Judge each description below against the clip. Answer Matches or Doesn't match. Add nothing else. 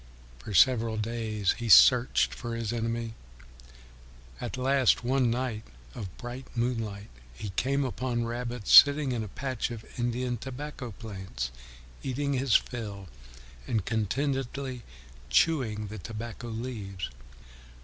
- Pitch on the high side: Doesn't match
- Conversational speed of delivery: Doesn't match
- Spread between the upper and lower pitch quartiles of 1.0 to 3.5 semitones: Matches